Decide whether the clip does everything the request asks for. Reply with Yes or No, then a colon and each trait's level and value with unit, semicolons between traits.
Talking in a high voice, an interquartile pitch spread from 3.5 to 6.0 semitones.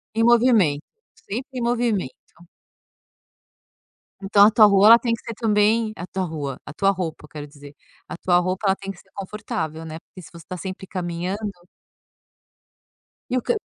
Yes: high, 195 Hz; average, 4.6 semitones